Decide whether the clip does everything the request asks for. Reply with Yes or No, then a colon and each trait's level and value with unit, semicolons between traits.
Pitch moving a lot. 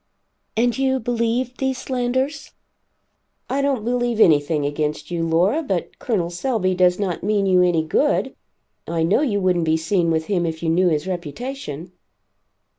Yes: wide, 6.8 semitones